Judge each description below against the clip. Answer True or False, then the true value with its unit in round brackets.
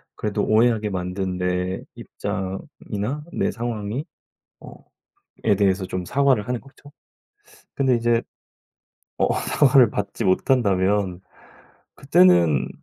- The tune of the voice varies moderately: True (4.4 semitones)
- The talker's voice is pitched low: True (105 Hz)